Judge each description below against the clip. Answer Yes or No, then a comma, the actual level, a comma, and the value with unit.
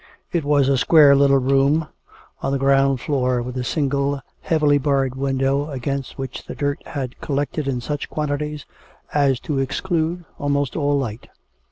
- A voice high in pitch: No, medium, 140 Hz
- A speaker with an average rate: Yes, average, 160 wpm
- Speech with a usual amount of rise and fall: No, narrow, 1.5 semitones